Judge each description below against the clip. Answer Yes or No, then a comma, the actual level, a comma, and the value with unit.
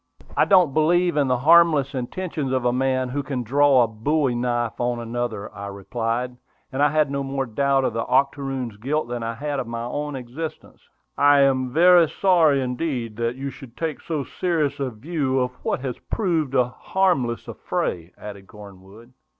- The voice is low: Yes, low, 130 Hz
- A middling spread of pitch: Yes, average, 3.7 semitones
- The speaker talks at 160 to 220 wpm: Yes, average, 185 wpm